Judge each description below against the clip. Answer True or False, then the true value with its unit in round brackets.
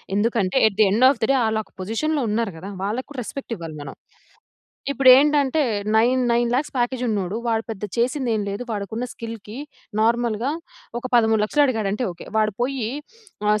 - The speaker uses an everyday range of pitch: True (3.4 semitones)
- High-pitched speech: True (225 Hz)